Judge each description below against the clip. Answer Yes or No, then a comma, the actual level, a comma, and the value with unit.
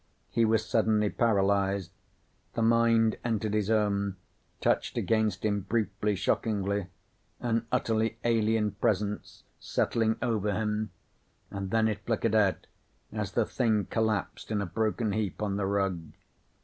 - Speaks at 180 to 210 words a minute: No, slow, 135 wpm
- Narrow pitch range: Yes, narrow, 1.9 semitones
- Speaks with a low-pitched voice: Yes, low, 105 Hz